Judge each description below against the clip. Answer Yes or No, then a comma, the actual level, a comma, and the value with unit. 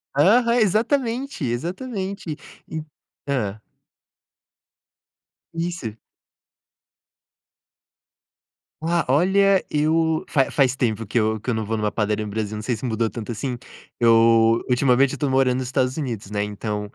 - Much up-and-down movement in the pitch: Yes, wide, 6.9 semitones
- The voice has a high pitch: No, low, 130 Hz